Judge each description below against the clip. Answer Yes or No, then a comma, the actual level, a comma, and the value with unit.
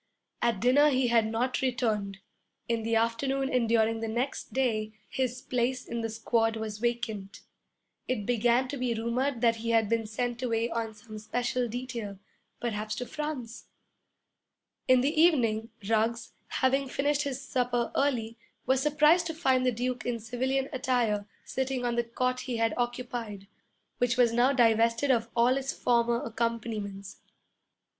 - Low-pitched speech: No, high, 240 Hz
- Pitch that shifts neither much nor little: No, narrow, 2.2 semitones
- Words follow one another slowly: No, average, 155 wpm